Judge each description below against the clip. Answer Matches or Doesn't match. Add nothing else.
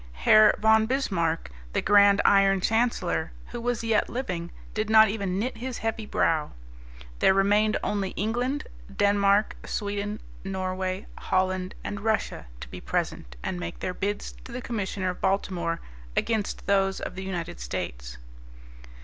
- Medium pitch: Doesn't match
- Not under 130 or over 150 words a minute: Matches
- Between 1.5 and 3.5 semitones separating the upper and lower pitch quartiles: Matches